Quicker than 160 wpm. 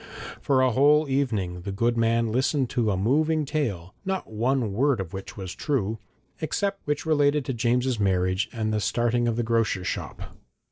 Yes: average, 185 wpm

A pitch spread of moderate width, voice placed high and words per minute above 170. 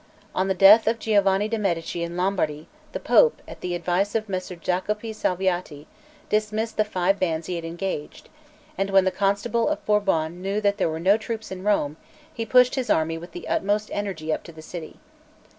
Yes: average, 3.5 semitones; high, 195 Hz; average, 195 wpm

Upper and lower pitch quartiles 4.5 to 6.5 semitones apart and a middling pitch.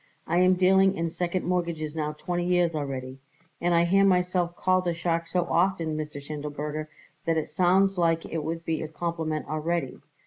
No: narrow, 2.5 semitones; medium, 170 Hz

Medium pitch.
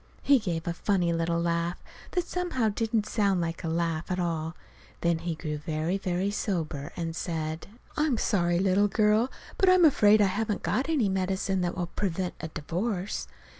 Yes: medium, 180 Hz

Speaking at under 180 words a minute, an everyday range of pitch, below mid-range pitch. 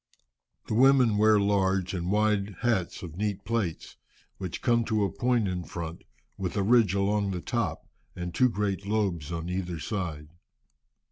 Yes: average, 160 wpm; average, 3.3 semitones; low, 100 Hz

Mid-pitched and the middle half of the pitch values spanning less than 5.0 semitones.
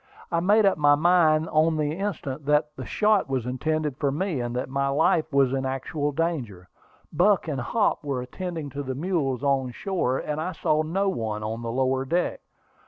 Yes: medium, 150 Hz; average, 4.1 semitones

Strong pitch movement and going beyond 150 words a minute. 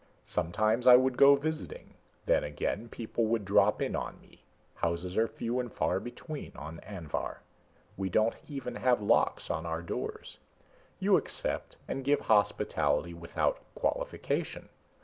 No: wide, 6.1 semitones; average, 145 wpm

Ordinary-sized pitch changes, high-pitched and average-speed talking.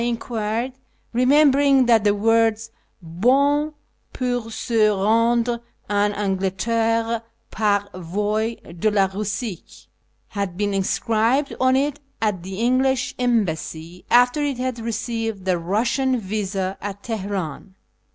No: average, 3.5 semitones; high, 225 Hz; slow, 120 wpm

